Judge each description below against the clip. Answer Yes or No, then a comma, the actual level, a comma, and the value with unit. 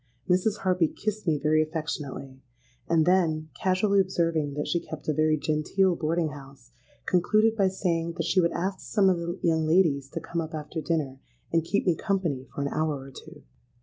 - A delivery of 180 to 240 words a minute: Yes, average, 190 wpm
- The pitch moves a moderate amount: Yes, average, 3.3 semitones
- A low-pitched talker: No, medium, 165 Hz